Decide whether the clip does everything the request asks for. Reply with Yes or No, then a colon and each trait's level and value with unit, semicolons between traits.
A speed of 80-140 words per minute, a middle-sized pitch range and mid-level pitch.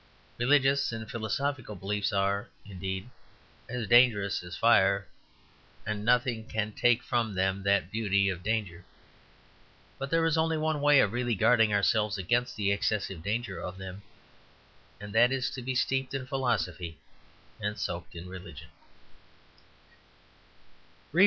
No: slow, 135 wpm; average, 4.0 semitones; low, 110 Hz